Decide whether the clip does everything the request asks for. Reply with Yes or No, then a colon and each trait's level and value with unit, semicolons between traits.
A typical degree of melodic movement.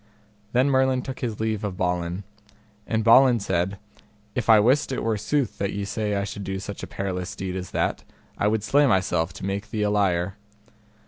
Yes: average, 3.1 semitones